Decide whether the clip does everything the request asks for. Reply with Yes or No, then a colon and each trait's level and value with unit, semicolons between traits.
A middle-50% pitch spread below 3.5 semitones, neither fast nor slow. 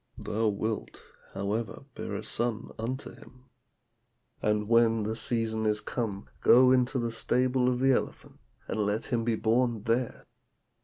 Yes: narrow, 2.4 semitones; average, 150 wpm